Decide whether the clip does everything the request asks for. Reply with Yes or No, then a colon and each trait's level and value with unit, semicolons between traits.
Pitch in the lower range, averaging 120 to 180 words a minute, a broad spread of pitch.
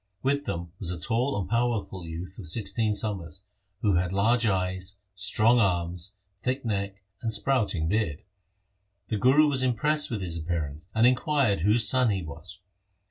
No: low, 100 Hz; average, 160 wpm; average, 5.0 semitones